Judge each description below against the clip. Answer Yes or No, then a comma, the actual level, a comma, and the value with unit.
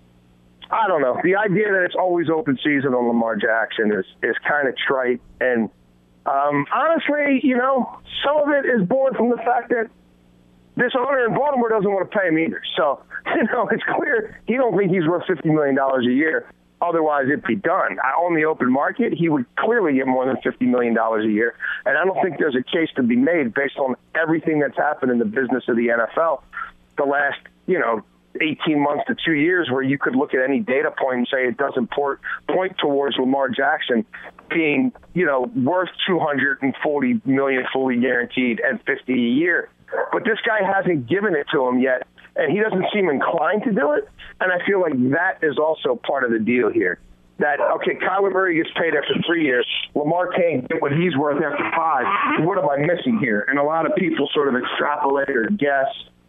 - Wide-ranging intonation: Yes, wide, 7.1 semitones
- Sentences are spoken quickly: Yes, fast, 210 wpm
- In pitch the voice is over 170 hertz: No, medium, 140 Hz